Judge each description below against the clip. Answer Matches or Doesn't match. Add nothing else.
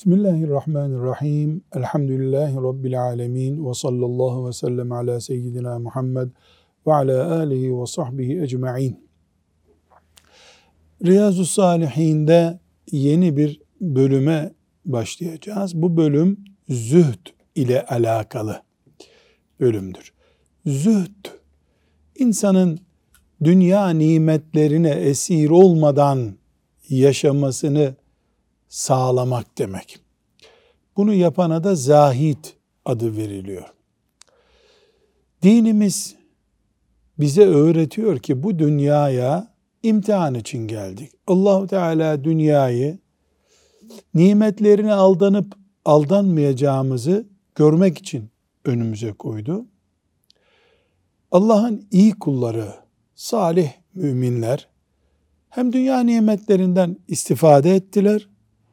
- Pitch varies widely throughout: Matches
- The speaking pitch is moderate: Matches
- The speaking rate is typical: Doesn't match